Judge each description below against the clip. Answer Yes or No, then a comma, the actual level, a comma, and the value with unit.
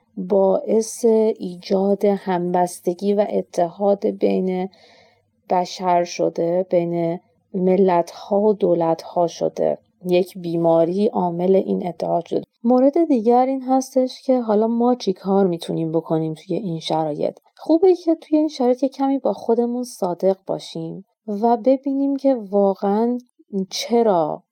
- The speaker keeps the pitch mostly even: No, average, 5.2 semitones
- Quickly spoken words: No, average, 125 wpm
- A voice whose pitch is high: Yes, high, 200 Hz